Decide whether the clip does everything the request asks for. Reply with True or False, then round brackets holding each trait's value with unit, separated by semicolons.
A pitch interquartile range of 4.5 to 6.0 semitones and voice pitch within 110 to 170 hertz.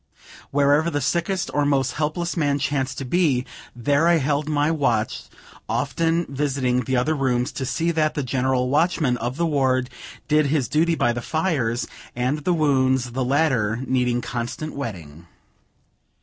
False (3.6 semitones; 140 Hz)